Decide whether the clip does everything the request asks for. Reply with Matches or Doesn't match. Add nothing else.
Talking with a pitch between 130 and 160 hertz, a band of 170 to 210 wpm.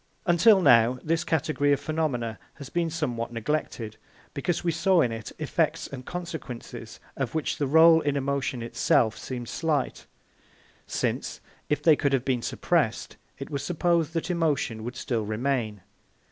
Doesn't match